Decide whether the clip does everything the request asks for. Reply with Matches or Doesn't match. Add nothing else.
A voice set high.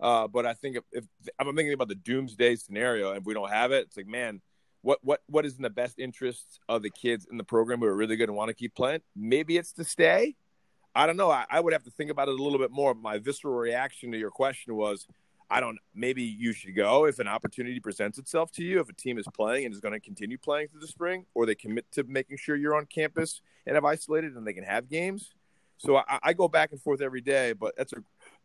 Doesn't match